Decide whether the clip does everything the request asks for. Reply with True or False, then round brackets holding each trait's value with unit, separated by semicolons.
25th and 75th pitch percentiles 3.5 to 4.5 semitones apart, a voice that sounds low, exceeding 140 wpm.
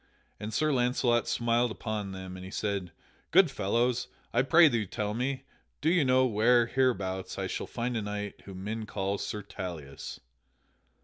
True (3.8 semitones; 110 Hz; 170 wpm)